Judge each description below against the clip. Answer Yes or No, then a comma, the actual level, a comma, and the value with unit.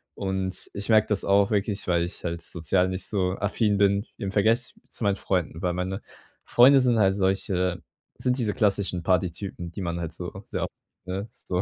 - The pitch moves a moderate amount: No, narrow, 2.1 semitones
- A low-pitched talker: Yes, very low, 95 Hz